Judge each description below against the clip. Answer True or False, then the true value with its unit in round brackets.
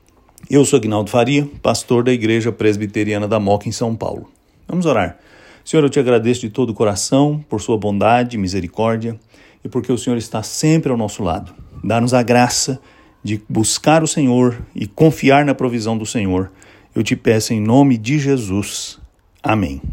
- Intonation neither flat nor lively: True (3.4 semitones)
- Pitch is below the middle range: True (115 Hz)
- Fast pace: False (175 wpm)